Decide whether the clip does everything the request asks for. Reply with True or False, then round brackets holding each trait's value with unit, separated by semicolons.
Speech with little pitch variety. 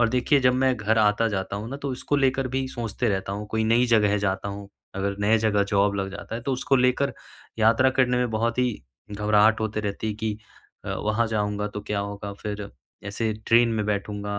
False (3.0 semitones)